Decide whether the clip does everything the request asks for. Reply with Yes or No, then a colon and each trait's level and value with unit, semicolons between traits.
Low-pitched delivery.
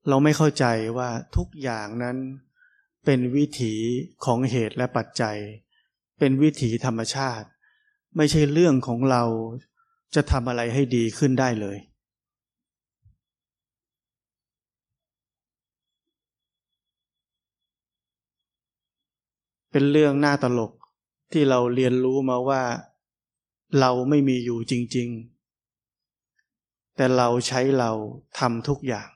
Yes: low, 125 Hz